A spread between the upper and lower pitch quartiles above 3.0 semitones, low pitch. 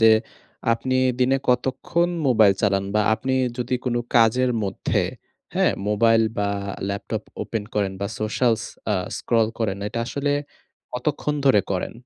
Yes: average, 3.6 semitones; low, 115 Hz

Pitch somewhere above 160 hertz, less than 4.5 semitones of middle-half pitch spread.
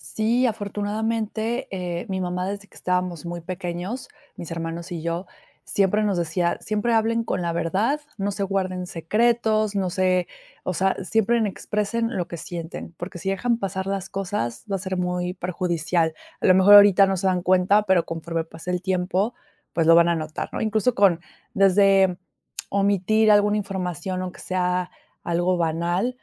Yes: medium, 185 Hz; average, 2.7 semitones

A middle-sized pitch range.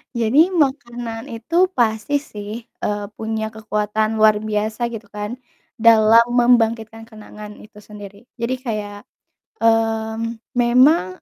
No: narrow, 1.7 semitones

